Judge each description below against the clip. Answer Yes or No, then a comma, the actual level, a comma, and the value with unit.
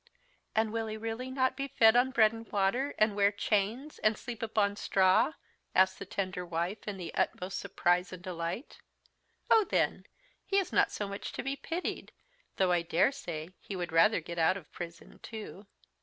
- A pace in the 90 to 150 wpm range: No, average, 185 wpm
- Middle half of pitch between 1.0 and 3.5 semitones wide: No, average, 3.9 semitones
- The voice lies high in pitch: Yes, high, 205 Hz